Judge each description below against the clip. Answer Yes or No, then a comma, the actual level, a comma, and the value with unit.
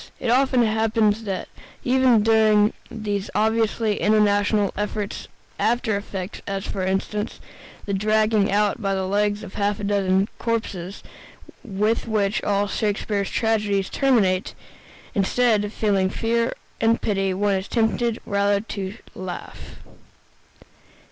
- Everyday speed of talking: No, slow, 125 wpm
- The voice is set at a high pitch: Yes, high, 210 Hz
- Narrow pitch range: Yes, narrow, 2.0 semitones